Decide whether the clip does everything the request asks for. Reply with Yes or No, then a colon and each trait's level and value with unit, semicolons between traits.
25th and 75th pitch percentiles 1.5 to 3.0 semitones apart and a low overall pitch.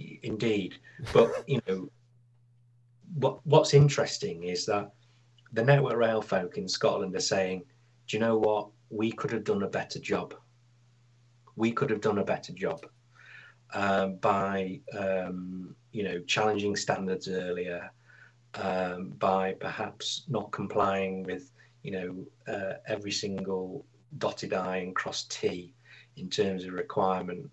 No: average, 4.3 semitones; low, 105 Hz